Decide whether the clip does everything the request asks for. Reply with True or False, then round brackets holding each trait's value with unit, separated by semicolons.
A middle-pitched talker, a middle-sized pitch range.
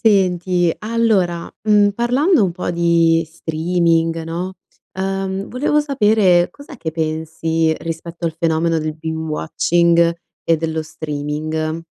True (170 Hz; 3.1 semitones)